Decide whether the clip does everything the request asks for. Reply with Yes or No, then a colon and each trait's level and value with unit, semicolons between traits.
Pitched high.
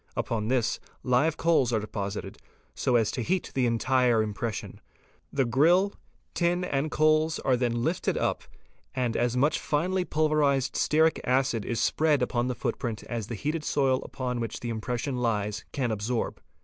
No: low, 125 Hz